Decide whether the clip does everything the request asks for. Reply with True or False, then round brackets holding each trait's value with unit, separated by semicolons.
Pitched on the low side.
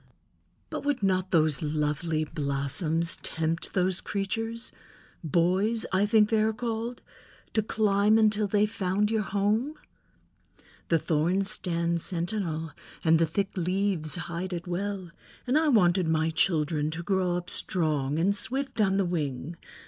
False (185 Hz)